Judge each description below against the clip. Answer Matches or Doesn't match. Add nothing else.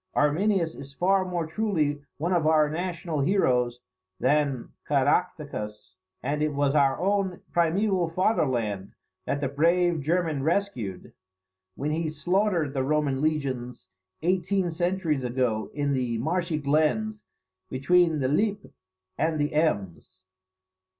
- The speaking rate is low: Matches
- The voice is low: Doesn't match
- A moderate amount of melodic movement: Matches